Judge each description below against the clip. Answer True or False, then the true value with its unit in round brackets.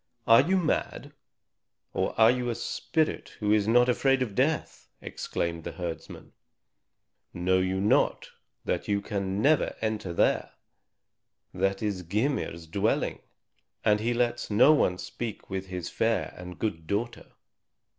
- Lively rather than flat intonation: False (4.6 semitones)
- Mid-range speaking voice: False (105 Hz)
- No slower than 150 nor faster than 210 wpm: False (140 wpm)